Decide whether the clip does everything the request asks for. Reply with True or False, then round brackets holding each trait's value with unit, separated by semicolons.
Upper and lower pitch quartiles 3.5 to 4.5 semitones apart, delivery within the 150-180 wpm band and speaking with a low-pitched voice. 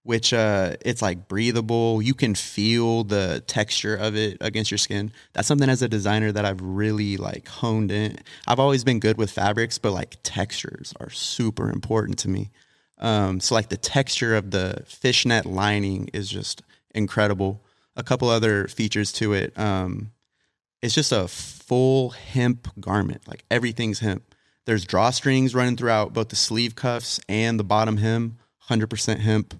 False (2.6 semitones; 165 wpm; 110 Hz)